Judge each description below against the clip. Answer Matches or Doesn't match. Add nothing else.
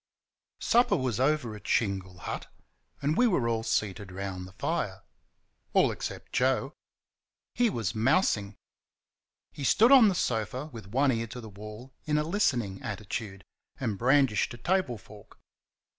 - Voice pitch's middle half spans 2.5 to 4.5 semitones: Doesn't match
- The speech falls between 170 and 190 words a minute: Doesn't match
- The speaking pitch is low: Matches